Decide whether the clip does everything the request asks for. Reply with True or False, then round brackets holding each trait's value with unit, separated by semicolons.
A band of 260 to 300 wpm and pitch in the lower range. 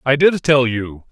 False (215 wpm; 130 Hz)